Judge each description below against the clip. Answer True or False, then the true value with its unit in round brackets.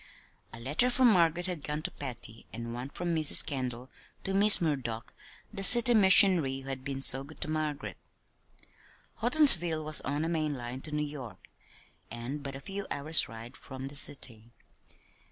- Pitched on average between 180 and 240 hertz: False (145 Hz)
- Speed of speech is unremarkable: True (170 wpm)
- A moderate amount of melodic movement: True (4.6 semitones)